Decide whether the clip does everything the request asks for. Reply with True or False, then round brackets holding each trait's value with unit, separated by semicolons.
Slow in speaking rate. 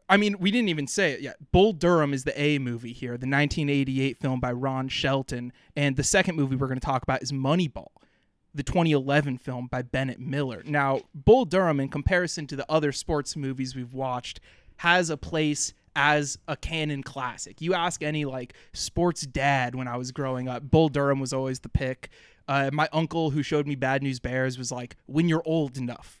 False (205 wpm)